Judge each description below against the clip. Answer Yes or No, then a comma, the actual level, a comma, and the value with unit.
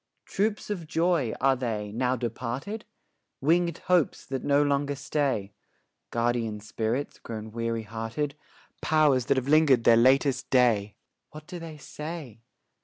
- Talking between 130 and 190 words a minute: Yes, slow, 135 wpm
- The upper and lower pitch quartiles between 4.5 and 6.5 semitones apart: Yes, average, 4.8 semitones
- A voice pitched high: No, low, 130 Hz